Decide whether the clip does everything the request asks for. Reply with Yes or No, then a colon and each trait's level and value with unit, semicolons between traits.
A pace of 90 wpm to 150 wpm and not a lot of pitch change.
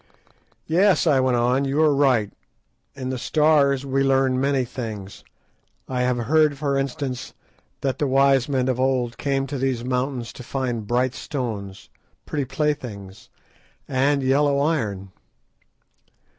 Yes: average, 140 wpm; narrow, 2.2 semitones